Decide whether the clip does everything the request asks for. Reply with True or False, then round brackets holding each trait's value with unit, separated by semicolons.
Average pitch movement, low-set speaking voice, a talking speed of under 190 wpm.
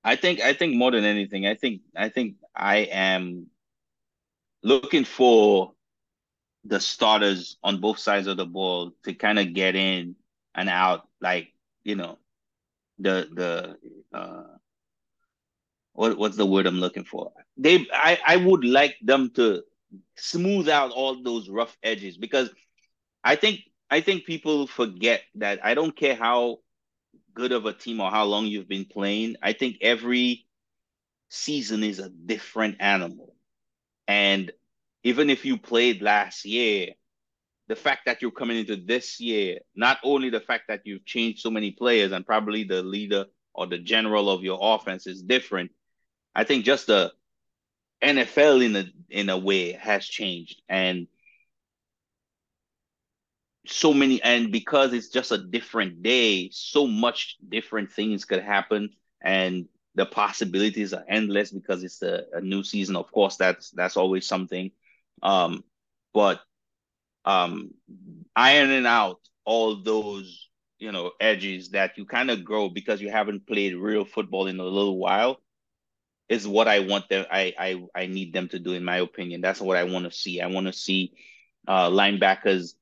True (3.8 semitones; 105 Hz; 160 wpm)